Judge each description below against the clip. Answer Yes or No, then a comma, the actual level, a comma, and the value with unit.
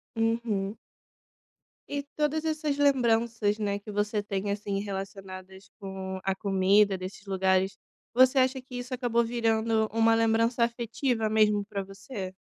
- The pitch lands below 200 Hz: No, high, 215 Hz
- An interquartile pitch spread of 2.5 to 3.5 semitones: Yes, average, 3.2 semitones